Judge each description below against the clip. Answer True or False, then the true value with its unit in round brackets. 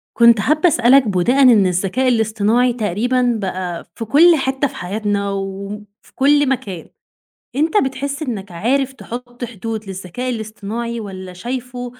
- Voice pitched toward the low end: False (235 Hz)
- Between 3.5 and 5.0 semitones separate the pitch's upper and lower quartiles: True (4.3 semitones)